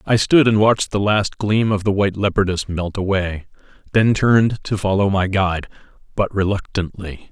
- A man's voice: Yes, male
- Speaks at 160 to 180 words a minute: Yes, average, 165 wpm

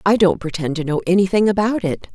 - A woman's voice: Yes, female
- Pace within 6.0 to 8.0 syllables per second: Yes, 6.1 syllables/s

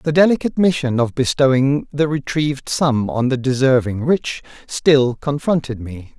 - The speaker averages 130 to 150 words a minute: Yes, average, 145 wpm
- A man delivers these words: Yes, male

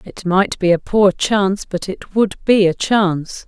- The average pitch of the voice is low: No, high, 190 Hz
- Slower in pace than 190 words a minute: No, fast, 205 wpm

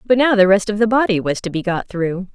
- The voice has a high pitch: Yes, high, 200 Hz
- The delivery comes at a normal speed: No, fast, 305 wpm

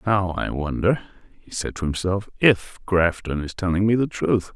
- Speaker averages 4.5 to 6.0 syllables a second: Yes, 4.7 syllables/s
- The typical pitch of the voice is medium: No, very low, 95 Hz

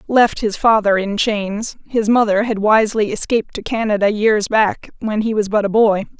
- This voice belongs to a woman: Yes, female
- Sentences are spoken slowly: No, average, 195 wpm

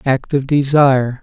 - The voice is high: No, low, 135 Hz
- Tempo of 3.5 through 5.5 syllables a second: Yes, 4.5 syllables/s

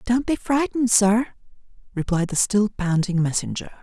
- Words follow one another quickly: No, average, 140 wpm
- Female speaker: No, male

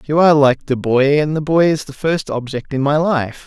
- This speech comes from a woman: No, male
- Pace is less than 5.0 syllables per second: No, 5.1 syllables/s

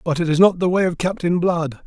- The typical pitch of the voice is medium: Yes, medium, 170 Hz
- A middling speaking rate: No, fast, 290 wpm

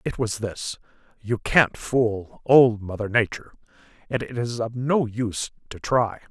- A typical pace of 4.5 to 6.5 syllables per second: No, 4.2 syllables/s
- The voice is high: No, low, 115 Hz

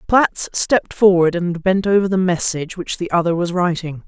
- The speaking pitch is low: No, medium, 180 Hz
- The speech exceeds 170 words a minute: Yes, average, 190 wpm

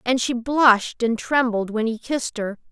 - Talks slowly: No, average, 200 wpm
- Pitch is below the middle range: No, high, 235 Hz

